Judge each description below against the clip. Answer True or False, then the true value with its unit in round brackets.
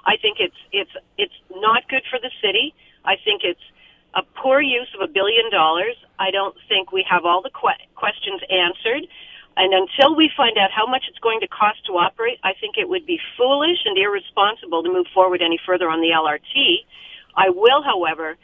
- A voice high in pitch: True (240 Hz)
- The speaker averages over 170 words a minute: True (200 wpm)